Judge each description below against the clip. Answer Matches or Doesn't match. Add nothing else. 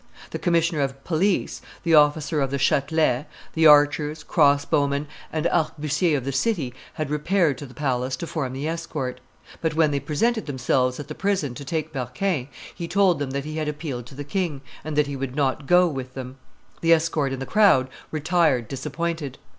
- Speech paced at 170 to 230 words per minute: Matches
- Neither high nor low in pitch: Matches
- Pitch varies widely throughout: Doesn't match